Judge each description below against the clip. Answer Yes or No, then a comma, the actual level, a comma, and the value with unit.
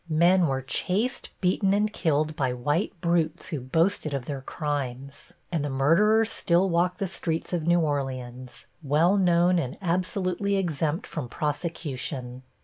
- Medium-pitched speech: Yes, medium, 160 Hz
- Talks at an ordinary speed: Yes, average, 145 wpm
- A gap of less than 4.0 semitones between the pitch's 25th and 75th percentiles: No, average, 4.7 semitones